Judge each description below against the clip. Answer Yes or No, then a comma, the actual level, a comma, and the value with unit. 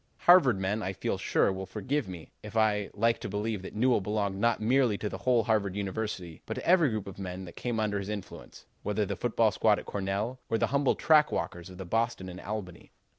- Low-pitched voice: Yes, low, 105 Hz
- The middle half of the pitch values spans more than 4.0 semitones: No, average, 3.2 semitones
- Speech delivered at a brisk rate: Yes, fast, 230 wpm